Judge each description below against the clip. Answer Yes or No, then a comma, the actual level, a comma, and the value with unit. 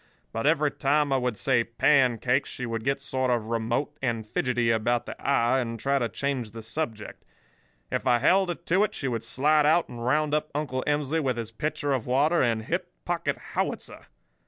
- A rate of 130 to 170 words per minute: No, average, 200 wpm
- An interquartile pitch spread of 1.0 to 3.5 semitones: No, average, 4.0 semitones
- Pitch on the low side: Yes, low, 130 Hz